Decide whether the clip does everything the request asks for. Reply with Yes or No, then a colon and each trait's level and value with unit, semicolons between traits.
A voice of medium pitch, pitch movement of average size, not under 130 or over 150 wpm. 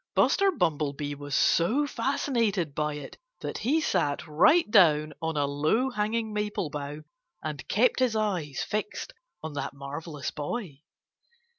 No: medium, 160 Hz; wide, 7.4 semitones; average, 140 wpm